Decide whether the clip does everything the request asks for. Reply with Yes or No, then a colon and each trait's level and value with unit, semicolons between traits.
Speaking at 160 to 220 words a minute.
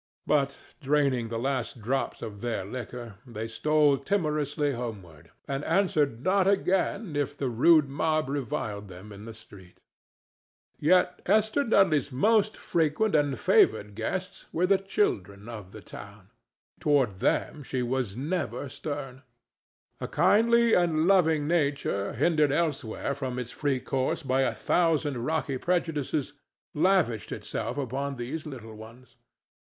No: slow, 135 wpm